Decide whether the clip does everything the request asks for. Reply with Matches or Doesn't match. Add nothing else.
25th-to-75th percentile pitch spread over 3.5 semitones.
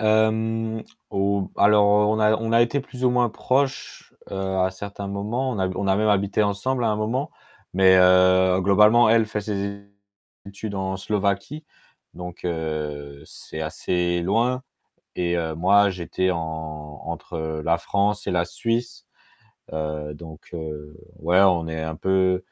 Matches